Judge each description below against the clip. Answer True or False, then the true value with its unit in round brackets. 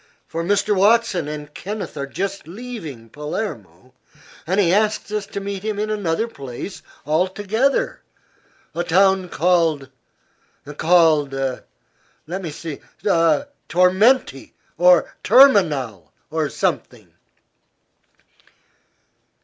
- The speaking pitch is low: False (180 Hz)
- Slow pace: True (100 wpm)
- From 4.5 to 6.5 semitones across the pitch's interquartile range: True (5.3 semitones)